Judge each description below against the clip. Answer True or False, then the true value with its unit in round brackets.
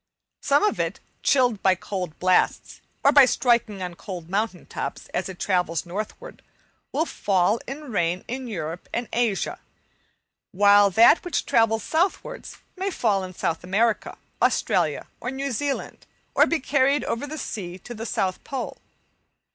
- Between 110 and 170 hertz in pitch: False (220 Hz)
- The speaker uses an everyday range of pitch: False (6.4 semitones)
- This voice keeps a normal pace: True (155 wpm)